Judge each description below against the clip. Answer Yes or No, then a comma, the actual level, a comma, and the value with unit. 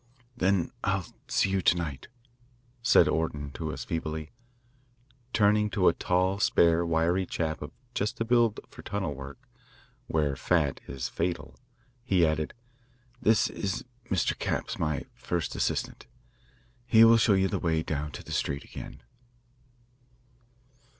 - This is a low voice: Yes, very low, 85 Hz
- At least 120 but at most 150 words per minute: Yes, average, 140 wpm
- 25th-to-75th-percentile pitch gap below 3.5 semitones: No, average, 4.2 semitones